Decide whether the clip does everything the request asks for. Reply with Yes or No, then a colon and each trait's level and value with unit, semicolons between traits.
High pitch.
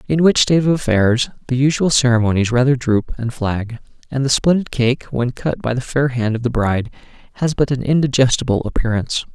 No: low, 125 Hz